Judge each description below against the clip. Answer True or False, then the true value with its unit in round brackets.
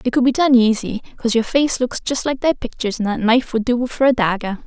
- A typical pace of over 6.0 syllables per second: True (6.2 syllables/s)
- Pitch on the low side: False (240 Hz)